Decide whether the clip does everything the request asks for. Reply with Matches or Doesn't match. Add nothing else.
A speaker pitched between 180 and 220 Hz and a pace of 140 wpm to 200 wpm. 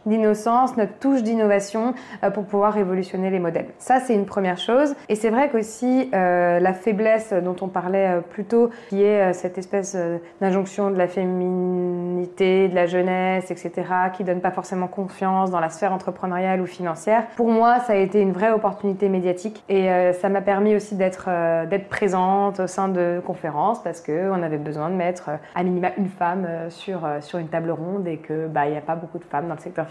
Doesn't match